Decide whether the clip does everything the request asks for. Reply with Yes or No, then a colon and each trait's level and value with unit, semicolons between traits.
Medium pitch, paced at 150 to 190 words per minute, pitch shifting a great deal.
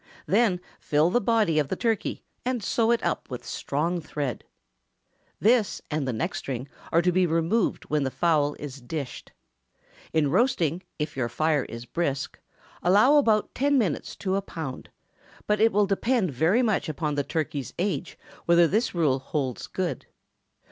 Yes: medium, 170 Hz; average, 165 wpm; wide, 6.4 semitones